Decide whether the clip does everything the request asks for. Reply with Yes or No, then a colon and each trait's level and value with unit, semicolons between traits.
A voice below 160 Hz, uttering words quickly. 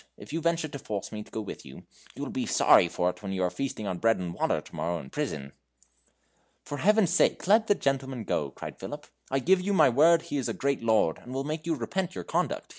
Yes: low, 135 Hz; fast, 250 wpm